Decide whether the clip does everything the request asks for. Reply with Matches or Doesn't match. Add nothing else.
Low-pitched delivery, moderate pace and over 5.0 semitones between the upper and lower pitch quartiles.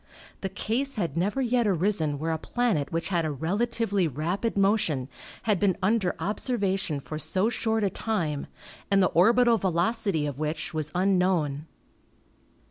Doesn't match